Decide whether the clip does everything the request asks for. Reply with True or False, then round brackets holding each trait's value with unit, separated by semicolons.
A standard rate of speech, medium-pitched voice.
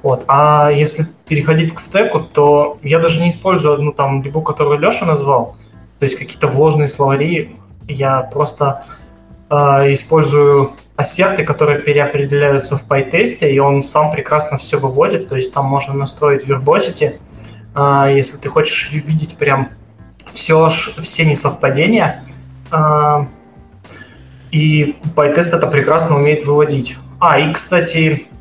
True (130 wpm; 145 Hz)